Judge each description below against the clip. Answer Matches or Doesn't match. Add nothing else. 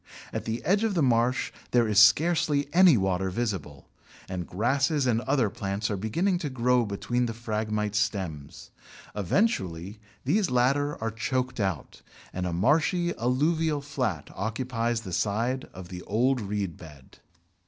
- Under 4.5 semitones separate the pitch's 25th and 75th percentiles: Doesn't match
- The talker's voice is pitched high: Doesn't match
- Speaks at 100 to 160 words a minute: Matches